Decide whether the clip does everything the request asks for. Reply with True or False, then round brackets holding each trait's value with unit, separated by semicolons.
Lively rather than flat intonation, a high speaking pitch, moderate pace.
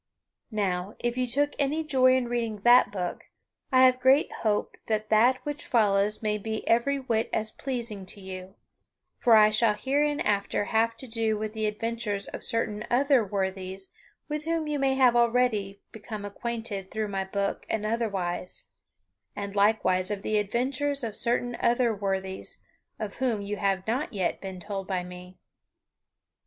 False (3.7 semitones; 220 Hz; 165 wpm)